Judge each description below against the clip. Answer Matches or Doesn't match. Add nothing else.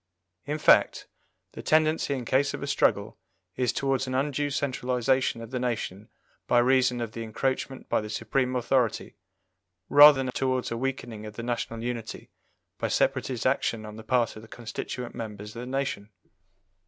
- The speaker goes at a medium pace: Matches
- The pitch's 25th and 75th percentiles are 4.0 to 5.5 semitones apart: Doesn't match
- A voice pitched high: Doesn't match